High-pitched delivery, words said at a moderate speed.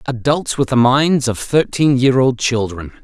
No: low, 130 Hz; average, 180 wpm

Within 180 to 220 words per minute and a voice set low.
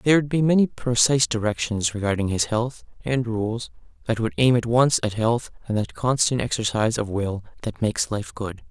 Yes: average, 195 wpm; low, 115 Hz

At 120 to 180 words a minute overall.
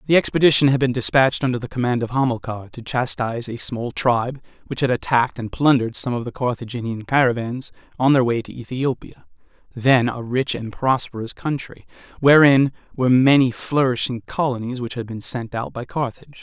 Yes: average, 175 wpm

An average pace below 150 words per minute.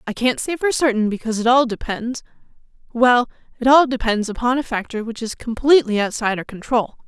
No: average, 180 wpm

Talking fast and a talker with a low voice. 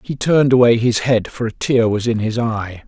Yes: fast, 250 wpm; low, 115 Hz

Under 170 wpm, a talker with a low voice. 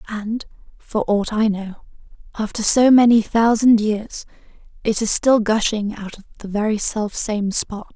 No: average, 150 wpm; high, 215 Hz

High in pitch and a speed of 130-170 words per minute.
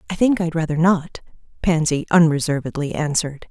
No: medium, 160 Hz; slow, 135 wpm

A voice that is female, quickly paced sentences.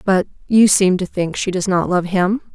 Yes: female; fast, 235 wpm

